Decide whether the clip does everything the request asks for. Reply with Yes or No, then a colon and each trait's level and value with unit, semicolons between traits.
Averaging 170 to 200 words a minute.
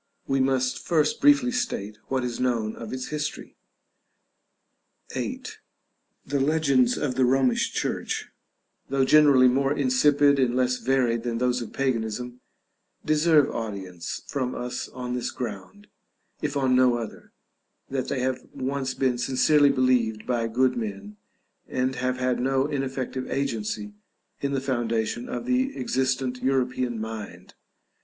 No: average, 140 wpm